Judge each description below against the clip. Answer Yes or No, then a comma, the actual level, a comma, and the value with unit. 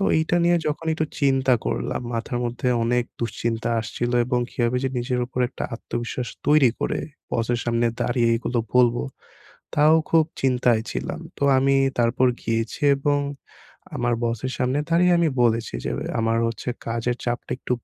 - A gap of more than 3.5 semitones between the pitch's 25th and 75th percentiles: No, narrow, 2.5 semitones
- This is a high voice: No, low, 120 Hz